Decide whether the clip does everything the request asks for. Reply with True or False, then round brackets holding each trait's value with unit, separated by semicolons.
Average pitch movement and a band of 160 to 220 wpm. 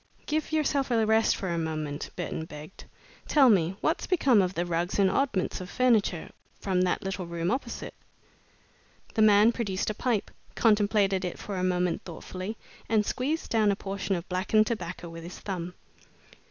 True (3.9 semitones; 170 wpm)